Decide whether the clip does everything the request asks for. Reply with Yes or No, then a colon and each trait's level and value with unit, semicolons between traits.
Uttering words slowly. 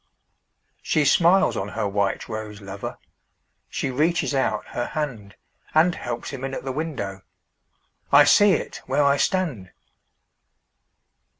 Yes: slow, 115 wpm